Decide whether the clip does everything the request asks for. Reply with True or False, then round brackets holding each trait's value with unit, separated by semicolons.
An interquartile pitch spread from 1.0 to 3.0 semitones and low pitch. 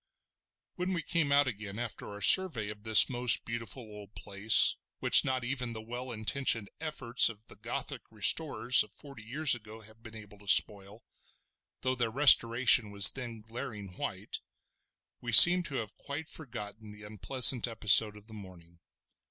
False (3.7 semitones; 115 Hz)